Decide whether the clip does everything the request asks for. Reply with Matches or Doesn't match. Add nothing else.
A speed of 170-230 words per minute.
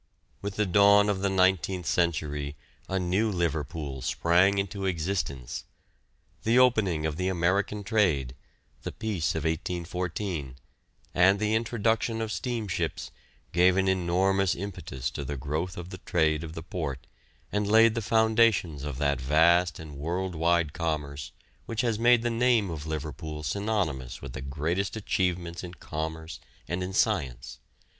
Doesn't match